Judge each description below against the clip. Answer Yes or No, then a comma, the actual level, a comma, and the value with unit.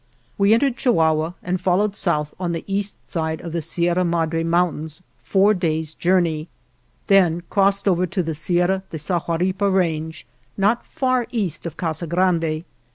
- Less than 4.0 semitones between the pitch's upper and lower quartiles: Yes, average, 3.1 semitones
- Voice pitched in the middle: Yes, medium, 175 Hz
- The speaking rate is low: No, average, 155 wpm